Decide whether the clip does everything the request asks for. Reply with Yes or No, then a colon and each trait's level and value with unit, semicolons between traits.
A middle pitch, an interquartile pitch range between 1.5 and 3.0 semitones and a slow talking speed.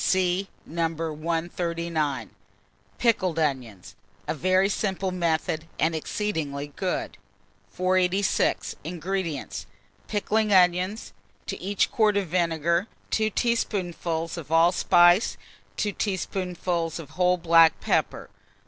Yes: medium, 175 Hz; average, 2.7 semitones; slow, 100 wpm